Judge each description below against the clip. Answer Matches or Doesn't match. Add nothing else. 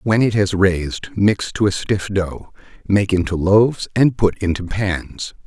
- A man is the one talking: Matches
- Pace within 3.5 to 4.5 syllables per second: Matches